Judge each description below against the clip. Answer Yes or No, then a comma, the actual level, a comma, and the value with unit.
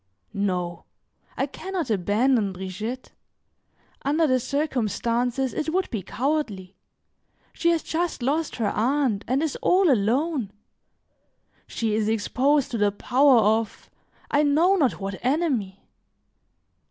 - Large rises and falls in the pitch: Yes, wide, 6.0 semitones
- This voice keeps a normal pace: No, slow, 125 wpm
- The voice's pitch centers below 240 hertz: No, very high, 250 Hz